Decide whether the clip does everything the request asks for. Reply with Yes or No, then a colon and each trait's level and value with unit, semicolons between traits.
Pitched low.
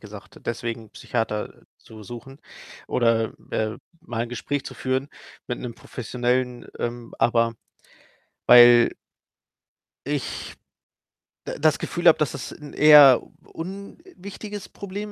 Yes: low, 125 Hz